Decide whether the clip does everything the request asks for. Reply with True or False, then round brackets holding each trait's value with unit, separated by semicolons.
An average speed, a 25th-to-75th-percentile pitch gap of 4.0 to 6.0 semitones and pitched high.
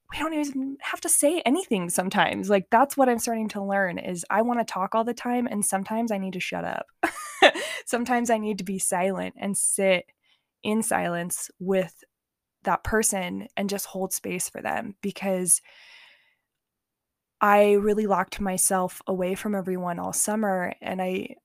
False (170 wpm; 3.4 semitones; 200 Hz)